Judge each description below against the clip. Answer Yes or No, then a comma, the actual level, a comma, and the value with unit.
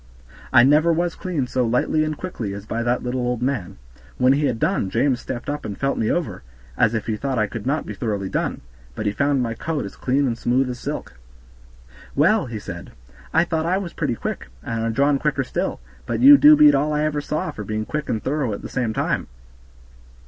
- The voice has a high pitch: No, low, 130 Hz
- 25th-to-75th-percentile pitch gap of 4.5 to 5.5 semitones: Yes, average, 5.0 semitones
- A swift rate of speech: Yes, fast, 230 wpm